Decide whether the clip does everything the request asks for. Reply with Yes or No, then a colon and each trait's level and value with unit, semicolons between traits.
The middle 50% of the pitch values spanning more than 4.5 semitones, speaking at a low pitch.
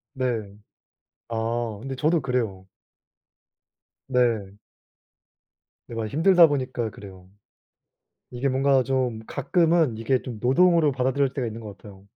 No: average, 3.7 semitones; low, 125 Hz